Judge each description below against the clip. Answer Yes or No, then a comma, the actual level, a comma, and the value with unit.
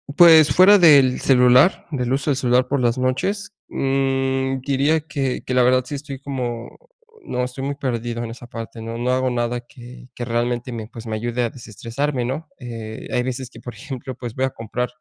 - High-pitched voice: No, low, 125 Hz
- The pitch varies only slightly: Yes, narrow, 2.2 semitones